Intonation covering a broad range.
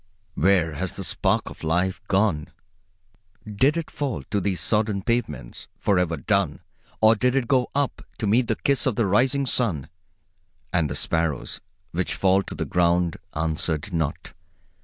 Yes: wide, 6.0 semitones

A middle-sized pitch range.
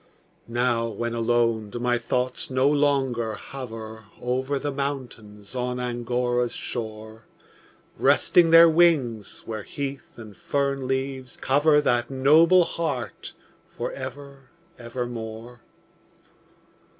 Yes: average, 3.0 semitones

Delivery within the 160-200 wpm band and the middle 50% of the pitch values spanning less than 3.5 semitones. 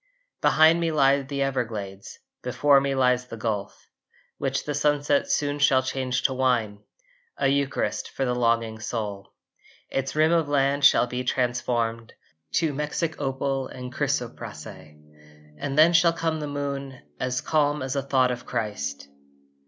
No: average, 150 wpm; average, 2.8 semitones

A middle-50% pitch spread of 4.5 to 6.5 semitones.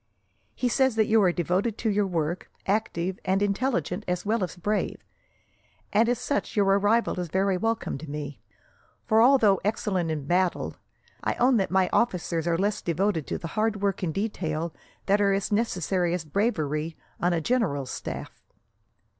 No: average, 4.1 semitones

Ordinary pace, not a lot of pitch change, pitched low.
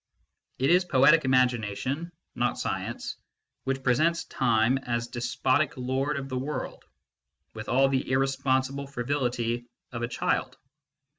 No: slow, 130 wpm; narrow, 2.1 semitones; low, 130 Hz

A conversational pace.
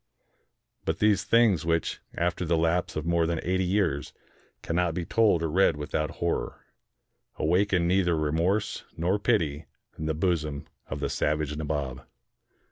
Yes: average, 145 wpm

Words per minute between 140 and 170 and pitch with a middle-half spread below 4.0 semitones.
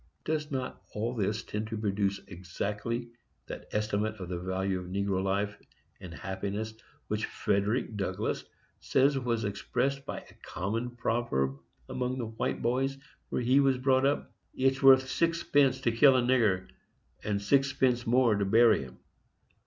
No: average, 155 wpm; average, 4.6 semitones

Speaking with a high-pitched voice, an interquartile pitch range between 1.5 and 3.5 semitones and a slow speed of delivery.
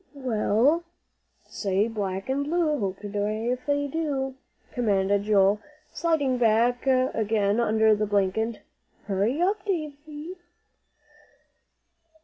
No: high, 225 Hz; average, 5.3 semitones; slow, 110 wpm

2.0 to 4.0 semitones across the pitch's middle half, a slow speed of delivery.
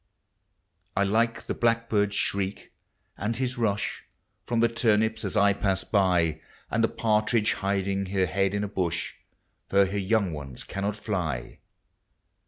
No: narrow, 2.5 semitones; average, 145 wpm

